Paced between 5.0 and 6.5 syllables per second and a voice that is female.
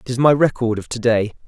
No: 6.0 syllables/s; male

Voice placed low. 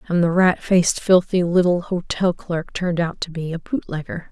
No: medium, 175 Hz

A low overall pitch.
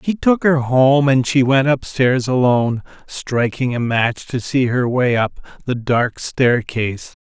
Yes: low, 130 Hz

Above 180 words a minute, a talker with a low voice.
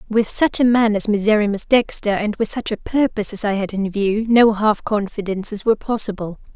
No: average, 200 wpm; high, 210 Hz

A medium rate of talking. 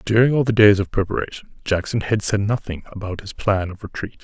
No: fast, 215 wpm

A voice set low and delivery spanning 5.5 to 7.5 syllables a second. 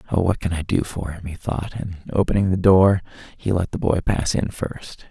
No: very low, 90 Hz; 5.2 syllables/s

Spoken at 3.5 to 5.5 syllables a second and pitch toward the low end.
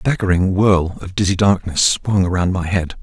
Yes: 5.0 syllables/s; very low, 95 Hz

